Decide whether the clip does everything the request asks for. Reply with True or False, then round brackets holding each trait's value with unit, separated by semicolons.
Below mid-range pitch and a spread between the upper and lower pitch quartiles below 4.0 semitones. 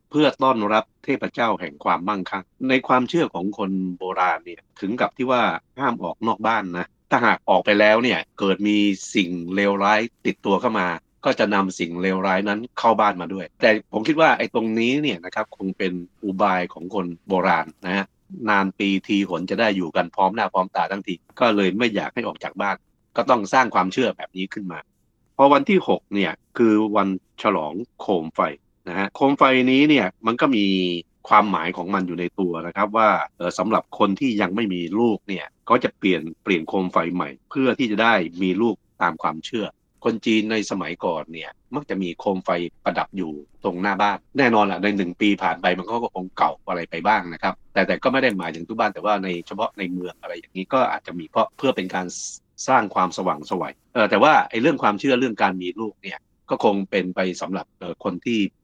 True (100 Hz; 2.8 semitones)